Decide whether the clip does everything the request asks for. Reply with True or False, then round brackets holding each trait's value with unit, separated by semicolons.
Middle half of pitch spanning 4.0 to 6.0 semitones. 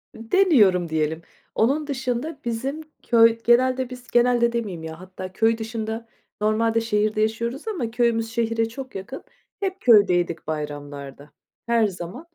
True (4.5 semitones)